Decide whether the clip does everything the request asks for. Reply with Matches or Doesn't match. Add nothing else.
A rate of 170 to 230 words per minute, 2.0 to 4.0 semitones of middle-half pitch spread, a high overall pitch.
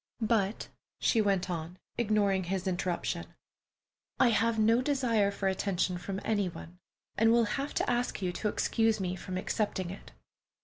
Doesn't match